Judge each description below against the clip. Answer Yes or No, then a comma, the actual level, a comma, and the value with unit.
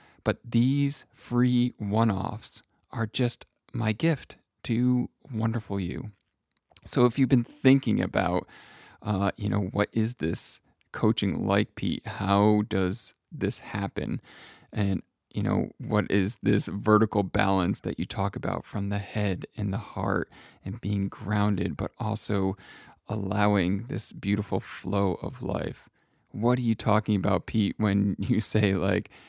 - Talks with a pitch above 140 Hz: No, low, 105 Hz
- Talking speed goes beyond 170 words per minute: No, average, 145 wpm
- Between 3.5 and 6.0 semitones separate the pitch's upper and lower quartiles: No, average, 2.8 semitones